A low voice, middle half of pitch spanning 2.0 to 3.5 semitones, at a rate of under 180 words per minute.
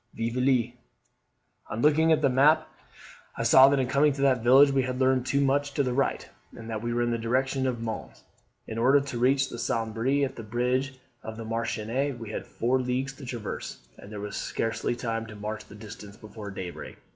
No: low, 125 Hz; average, 3.0 semitones; fast, 205 wpm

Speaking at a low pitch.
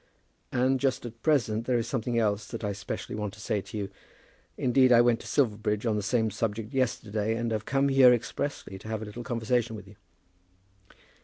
Yes: low, 115 Hz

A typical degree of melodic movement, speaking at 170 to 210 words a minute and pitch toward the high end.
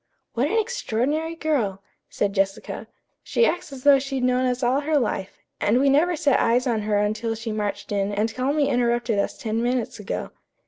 Yes: average, 4.6 semitones; average, 190 wpm; high, 245 Hz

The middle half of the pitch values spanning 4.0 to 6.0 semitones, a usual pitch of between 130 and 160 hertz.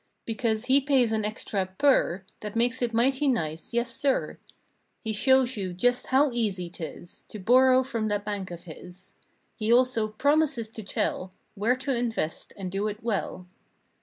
No: average, 4.4 semitones; high, 225 Hz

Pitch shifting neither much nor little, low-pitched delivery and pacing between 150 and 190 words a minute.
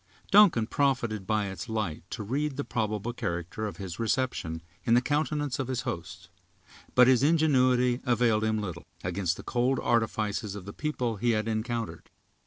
Yes: average, 4.0 semitones; low, 115 Hz; average, 170 wpm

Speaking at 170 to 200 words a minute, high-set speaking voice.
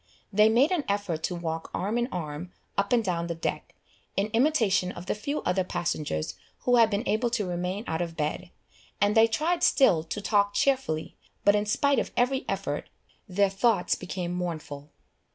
Yes: average, 185 wpm; high, 200 Hz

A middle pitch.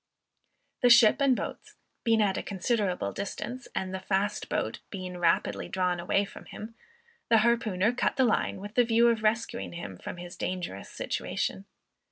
No: high, 205 Hz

